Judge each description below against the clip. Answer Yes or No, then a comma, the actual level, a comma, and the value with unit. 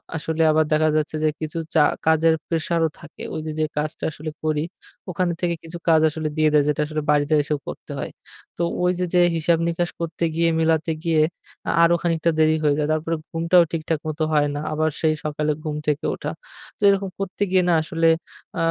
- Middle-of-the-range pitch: Yes, medium, 160 Hz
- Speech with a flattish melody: Yes, narrow, 1.4 semitones